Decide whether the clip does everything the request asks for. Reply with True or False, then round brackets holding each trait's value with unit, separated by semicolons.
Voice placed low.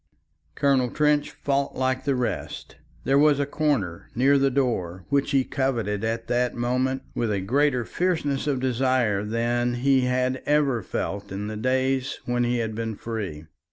True (125 Hz)